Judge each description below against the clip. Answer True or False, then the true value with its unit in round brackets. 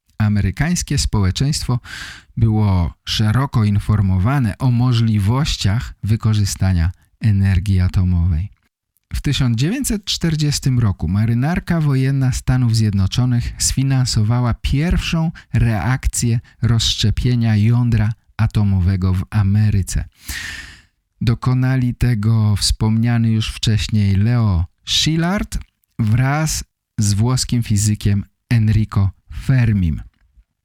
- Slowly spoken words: True (75 wpm)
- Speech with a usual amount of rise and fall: True (3.9 semitones)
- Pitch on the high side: False (110 Hz)